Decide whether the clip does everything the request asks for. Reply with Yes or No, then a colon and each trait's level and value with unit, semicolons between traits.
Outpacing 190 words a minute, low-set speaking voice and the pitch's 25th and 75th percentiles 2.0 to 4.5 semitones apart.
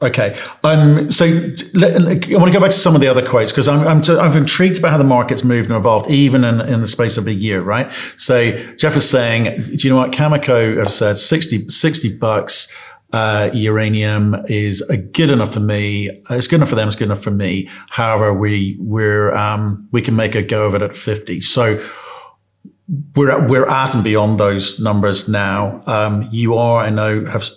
No: fast, 205 wpm; low, 115 Hz; average, 5.1 semitones